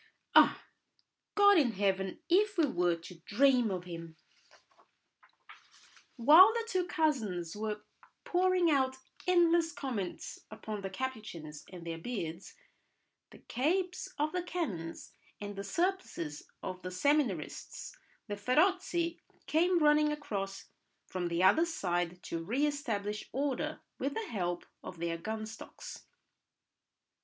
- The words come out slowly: Yes, slow, 130 wpm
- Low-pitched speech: No, high, 230 Hz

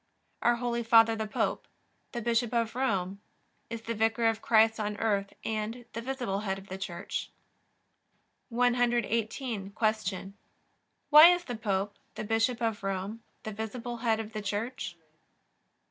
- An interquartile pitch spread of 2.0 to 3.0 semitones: Yes, narrow, 2.4 semitones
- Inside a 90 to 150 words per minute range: Yes, average, 145 wpm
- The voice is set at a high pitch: Yes, high, 225 Hz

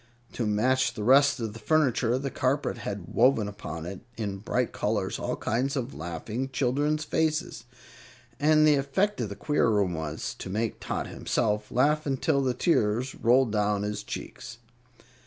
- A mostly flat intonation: No, average, 4.8 semitones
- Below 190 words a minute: Yes, average, 165 wpm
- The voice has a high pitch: No, low, 120 Hz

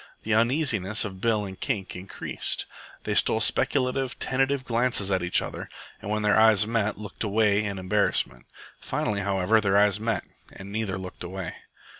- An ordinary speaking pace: Yes, average, 165 wpm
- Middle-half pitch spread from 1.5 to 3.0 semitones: Yes, narrow, 2.6 semitones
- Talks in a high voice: No, low, 105 Hz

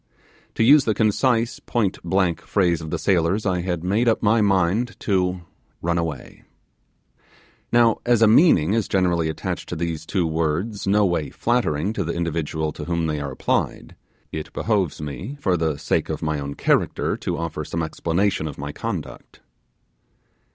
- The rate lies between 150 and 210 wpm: Yes, average, 165 wpm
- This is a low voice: Yes, very low, 90 Hz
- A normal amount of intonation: Yes, average, 4.7 semitones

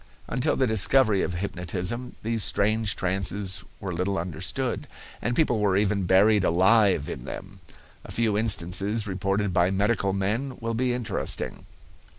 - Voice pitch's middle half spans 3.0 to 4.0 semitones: Yes, average, 3.3 semitones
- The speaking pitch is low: Yes, low, 100 Hz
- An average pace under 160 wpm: Yes, average, 145 wpm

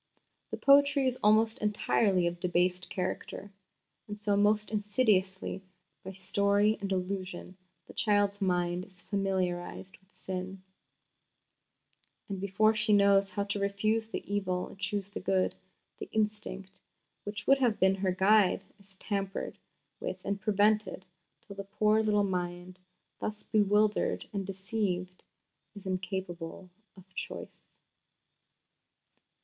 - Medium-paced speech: No, slow, 130 wpm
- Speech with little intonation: Yes, narrow, 2.0 semitones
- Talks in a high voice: Yes, high, 200 Hz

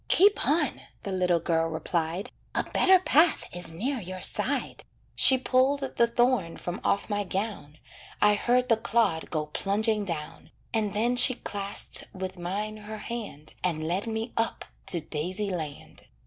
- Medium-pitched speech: No, high, 205 Hz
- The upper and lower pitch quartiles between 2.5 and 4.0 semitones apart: No, average, 5.3 semitones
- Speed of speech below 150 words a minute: No, average, 160 wpm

